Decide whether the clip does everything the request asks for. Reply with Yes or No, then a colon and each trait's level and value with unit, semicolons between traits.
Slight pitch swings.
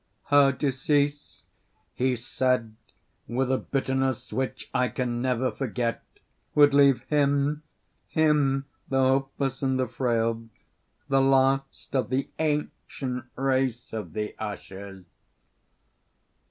Yes: narrow, 1.8 semitones